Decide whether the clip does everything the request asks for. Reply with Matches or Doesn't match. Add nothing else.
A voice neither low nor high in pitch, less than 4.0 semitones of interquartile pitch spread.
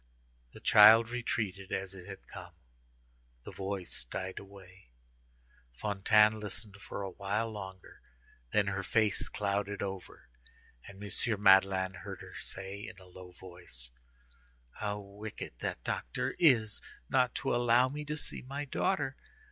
Doesn't match